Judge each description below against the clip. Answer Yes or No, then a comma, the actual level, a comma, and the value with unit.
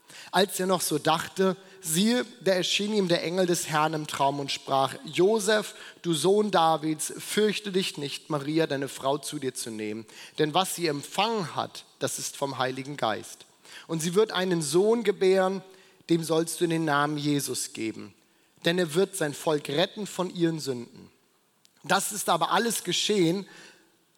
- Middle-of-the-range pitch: Yes, medium, 170 Hz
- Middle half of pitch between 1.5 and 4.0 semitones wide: No, average, 4.4 semitones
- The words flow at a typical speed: Yes, average, 170 wpm